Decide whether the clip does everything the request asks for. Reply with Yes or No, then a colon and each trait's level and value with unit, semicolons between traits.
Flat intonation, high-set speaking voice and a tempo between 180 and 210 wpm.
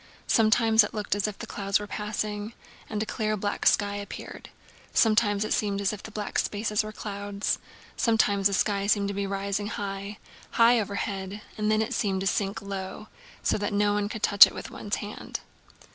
Yes: narrow, 1.2 semitones; high, 205 Hz; average, 190 wpm